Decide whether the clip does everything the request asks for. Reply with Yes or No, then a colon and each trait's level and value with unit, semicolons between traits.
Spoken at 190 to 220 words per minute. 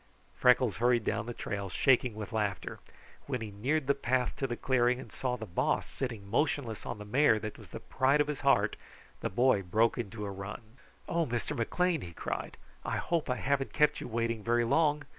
Yes: fast, 205 wpm